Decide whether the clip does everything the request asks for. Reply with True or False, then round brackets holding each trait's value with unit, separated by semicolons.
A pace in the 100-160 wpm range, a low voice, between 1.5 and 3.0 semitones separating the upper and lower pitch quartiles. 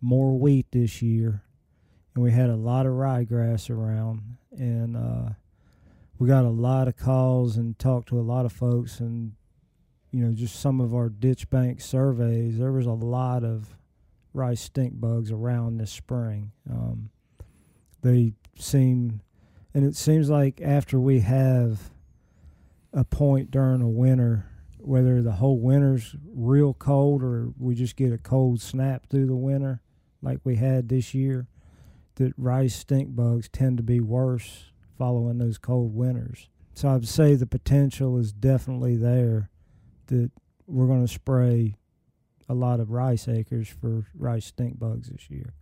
True (155 wpm; 120 Hz; 2.4 semitones)